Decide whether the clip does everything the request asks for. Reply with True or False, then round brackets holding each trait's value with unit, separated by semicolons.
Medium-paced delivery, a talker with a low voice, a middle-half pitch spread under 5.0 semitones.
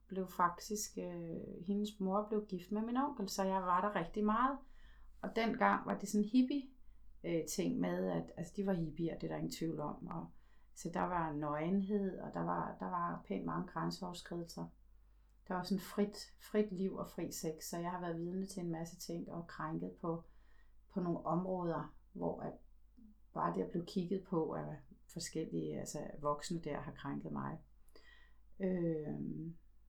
False (175 wpm; 180 Hz; 4.3 semitones)